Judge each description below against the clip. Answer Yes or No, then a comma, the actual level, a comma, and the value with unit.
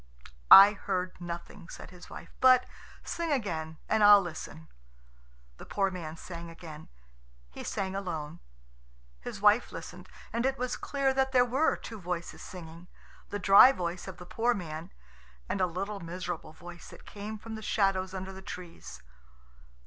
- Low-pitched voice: No, medium, 185 Hz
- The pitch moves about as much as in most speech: Yes, average, 4.0 semitones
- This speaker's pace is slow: No, average, 160 wpm